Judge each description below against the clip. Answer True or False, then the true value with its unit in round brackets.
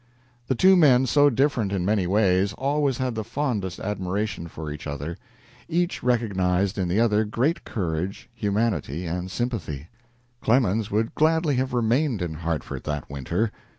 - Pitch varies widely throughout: True (5.8 semitones)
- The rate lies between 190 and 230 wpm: False (150 wpm)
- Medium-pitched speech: False (105 Hz)